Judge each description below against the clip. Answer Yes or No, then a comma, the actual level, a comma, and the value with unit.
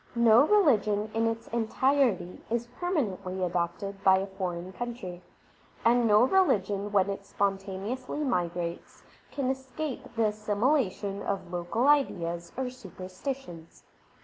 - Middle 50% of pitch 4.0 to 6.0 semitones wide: Yes, average, 5.2 semitones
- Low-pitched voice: No, high, 210 Hz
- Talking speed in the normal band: No, slow, 120 wpm